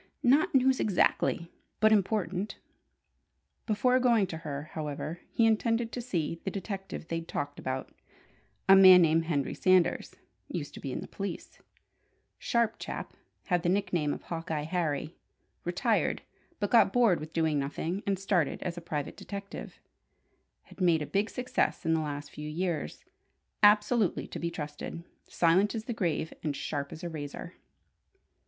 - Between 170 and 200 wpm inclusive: No, average, 155 wpm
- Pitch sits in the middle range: Yes, medium, 175 Hz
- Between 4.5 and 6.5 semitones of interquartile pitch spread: Yes, average, 4.8 semitones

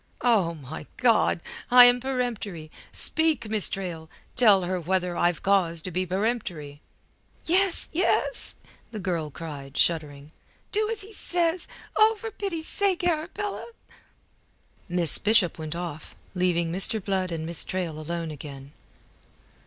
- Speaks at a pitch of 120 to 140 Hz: No, medium, 185 Hz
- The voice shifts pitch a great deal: Yes, wide, 7.3 semitones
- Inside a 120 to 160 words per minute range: Yes, slow, 135 wpm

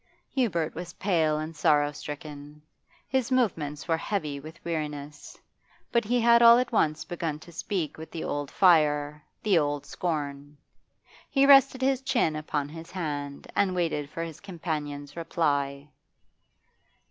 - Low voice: No, medium, 160 Hz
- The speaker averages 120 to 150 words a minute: Yes, average, 145 wpm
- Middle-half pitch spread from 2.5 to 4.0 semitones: No, average, 4.6 semitones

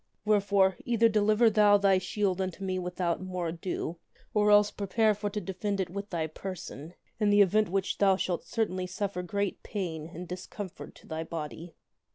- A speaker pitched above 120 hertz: Yes, high, 190 Hz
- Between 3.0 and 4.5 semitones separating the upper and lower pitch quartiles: No, narrow, 2.5 semitones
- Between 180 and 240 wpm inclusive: Yes, average, 185 wpm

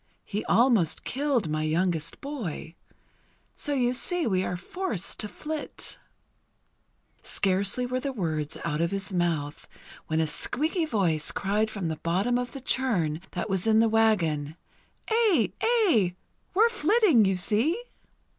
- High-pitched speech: Yes, high, 210 Hz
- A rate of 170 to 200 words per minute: No, average, 145 wpm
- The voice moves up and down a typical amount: No, wide, 7.7 semitones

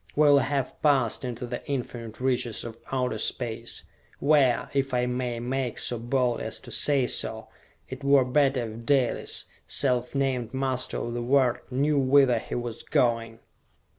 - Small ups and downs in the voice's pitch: Yes, narrow, 2.3 semitones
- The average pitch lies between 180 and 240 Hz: No, low, 125 Hz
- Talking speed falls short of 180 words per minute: Yes, average, 165 wpm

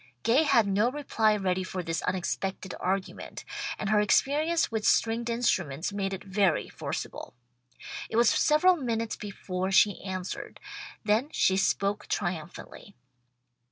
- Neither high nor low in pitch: No, high, 205 Hz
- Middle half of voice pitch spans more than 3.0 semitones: Yes, average, 3.6 semitones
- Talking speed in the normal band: No, slow, 130 wpm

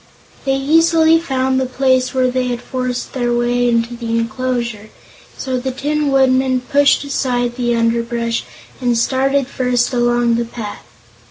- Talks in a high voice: Yes, very high, 250 Hz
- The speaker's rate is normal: Yes, average, 150 wpm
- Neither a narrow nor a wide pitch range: No, narrow, 1.9 semitones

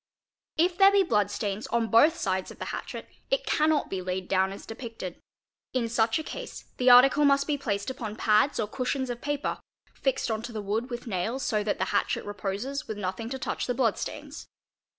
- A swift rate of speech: Yes, fast, 210 wpm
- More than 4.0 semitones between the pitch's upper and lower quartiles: Yes, average, 4.9 semitones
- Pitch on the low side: No, high, 230 Hz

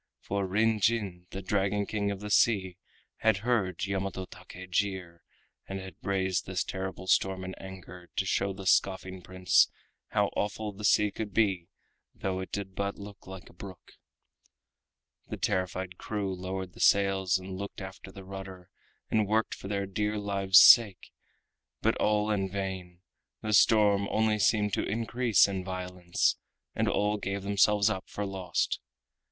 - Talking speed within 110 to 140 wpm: No, average, 160 wpm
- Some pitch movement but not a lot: No, narrow, 1.6 semitones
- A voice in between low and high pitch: No, very low, 95 Hz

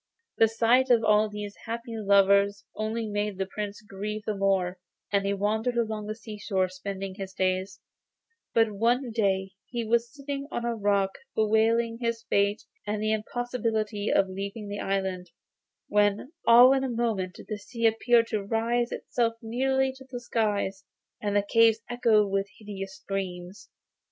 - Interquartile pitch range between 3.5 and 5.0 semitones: No, average, 2.7 semitones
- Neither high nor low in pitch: No, high, 215 Hz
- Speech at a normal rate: Yes, average, 160 wpm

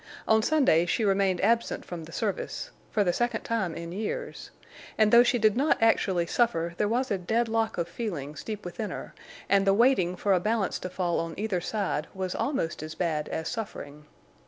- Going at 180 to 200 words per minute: Yes, average, 190 wpm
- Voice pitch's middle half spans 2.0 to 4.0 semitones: No, average, 4.7 semitones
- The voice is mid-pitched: No, high, 200 Hz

